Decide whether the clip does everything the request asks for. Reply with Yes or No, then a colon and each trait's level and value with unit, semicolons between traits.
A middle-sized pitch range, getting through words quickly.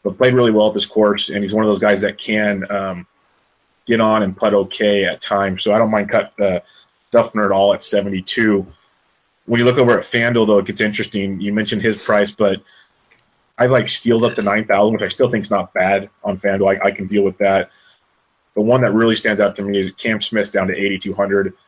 No: narrow, 1.5 semitones; fast, 235 wpm